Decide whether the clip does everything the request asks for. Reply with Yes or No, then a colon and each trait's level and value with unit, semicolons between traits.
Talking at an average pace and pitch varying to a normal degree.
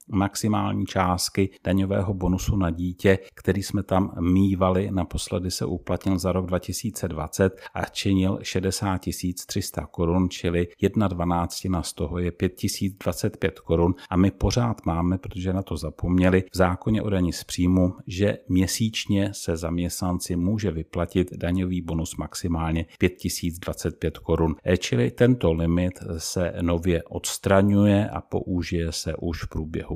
No: average, 130 wpm; narrow, 2.2 semitones